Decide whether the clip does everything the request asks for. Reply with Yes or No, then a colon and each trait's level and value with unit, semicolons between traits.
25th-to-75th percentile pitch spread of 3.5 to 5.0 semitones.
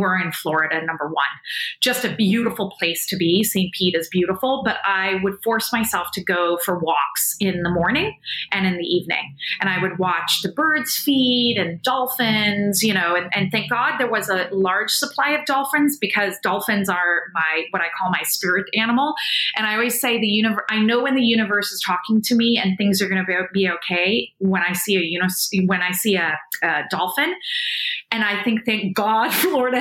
Yes: average, 4.2 semitones